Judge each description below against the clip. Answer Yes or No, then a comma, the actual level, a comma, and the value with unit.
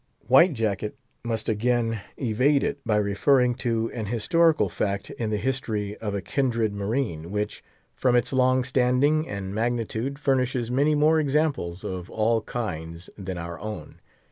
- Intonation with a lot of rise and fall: No, average, 4.1 semitones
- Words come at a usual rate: Yes, average, 150 wpm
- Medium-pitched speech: No, low, 115 Hz